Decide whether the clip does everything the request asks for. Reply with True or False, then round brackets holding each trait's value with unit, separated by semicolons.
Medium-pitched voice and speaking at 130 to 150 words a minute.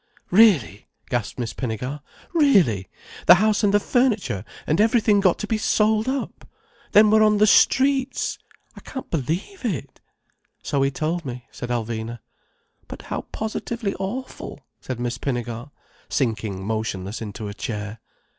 True (155 Hz; 145 wpm)